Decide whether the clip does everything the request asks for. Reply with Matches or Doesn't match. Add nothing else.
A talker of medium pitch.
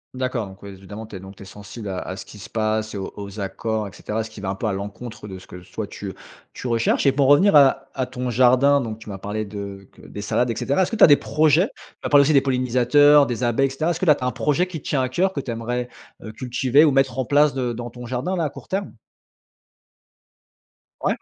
Doesn't match